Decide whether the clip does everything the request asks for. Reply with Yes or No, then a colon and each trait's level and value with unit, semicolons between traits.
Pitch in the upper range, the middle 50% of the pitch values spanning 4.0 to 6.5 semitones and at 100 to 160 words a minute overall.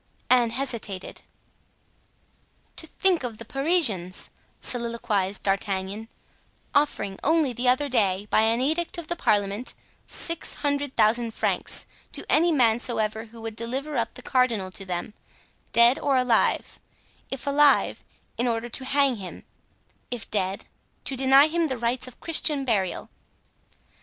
Yes: high, 240 Hz; average, 4.4 semitones; slow, 135 wpm